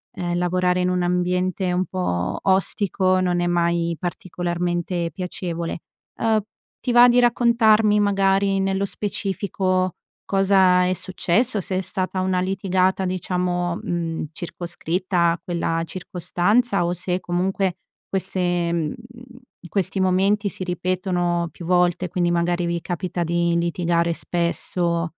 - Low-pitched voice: No, medium, 180 Hz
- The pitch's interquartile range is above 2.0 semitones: No, narrow, 1.7 semitones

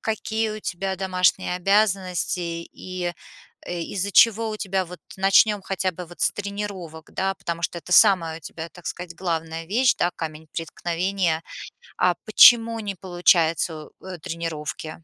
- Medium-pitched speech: Yes, medium, 180 Hz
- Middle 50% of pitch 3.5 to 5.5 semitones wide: No, average, 2.9 semitones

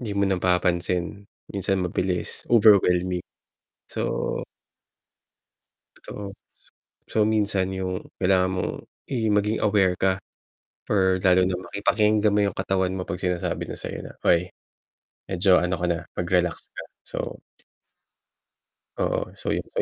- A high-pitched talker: No, very low, 95 Hz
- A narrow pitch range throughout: Yes, narrow, 1.9 semitones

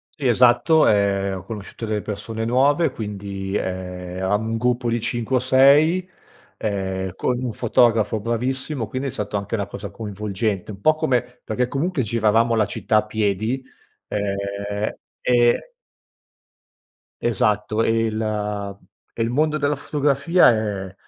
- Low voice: Yes, low, 110 Hz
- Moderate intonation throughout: Yes, average, 3.6 semitones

